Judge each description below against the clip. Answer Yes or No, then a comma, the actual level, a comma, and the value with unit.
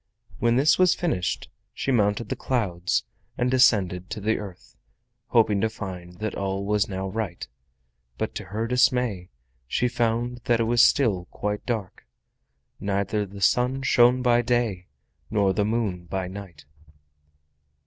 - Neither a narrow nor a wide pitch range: Yes, average, 4.0 semitones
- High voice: No, low, 105 Hz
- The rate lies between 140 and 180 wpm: Yes, average, 150 wpm